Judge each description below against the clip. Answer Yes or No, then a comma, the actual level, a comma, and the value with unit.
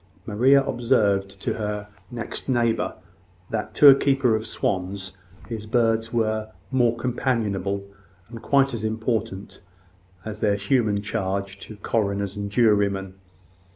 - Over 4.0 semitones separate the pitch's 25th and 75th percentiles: No, average, 2.8 semitones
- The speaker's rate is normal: No, slow, 125 wpm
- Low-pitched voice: Yes, low, 110 Hz